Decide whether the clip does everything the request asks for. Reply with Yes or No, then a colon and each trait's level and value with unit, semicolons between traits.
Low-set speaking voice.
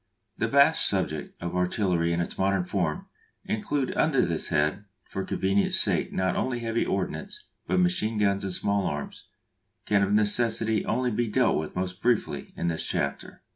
Yes: low, 100 Hz